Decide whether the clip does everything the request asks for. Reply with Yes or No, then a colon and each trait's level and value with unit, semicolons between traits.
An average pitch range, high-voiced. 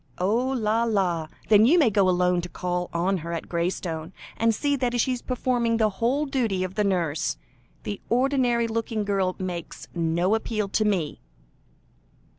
Yes: average, 4.7 semitones; high, 205 Hz